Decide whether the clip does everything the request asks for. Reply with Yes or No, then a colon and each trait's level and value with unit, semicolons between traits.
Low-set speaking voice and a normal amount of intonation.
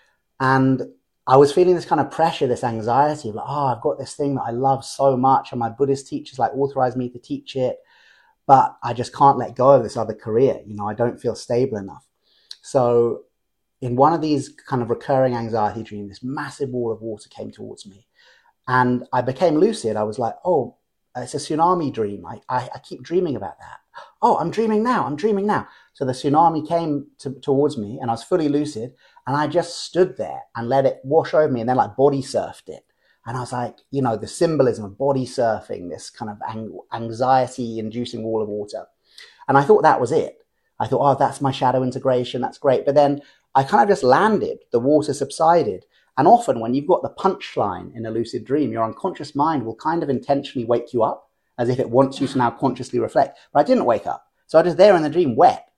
Yes: low, 130 Hz; average, 3.8 semitones